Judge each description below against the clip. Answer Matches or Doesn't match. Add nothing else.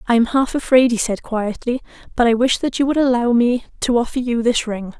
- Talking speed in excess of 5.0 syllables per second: Matches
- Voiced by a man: Doesn't match